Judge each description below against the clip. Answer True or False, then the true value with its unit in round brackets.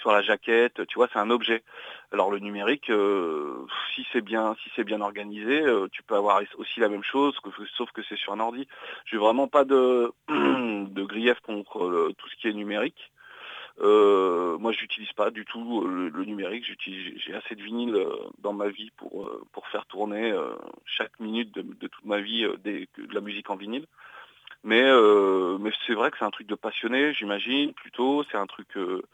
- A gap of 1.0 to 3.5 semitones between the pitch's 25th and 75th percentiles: False (5.0 semitones)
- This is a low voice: True (115 Hz)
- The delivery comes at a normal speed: True (200 wpm)